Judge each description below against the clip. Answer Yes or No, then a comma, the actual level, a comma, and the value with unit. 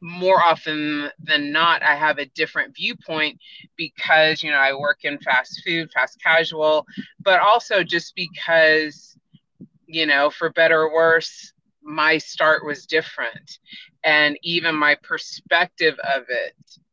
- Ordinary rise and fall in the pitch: No, narrow, 2.2 semitones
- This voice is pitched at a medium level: Yes, medium, 160 Hz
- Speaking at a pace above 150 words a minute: No, average, 140 wpm